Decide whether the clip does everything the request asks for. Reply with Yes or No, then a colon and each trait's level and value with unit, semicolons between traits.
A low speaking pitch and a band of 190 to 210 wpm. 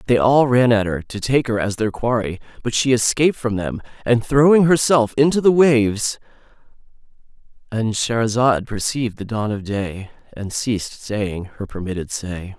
No: low, 115 Hz; average, 160 wpm